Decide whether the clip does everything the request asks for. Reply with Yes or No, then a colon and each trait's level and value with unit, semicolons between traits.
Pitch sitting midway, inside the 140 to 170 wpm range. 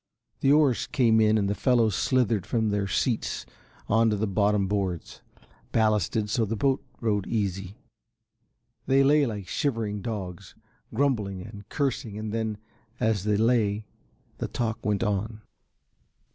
No: low, 110 Hz; average, 145 wpm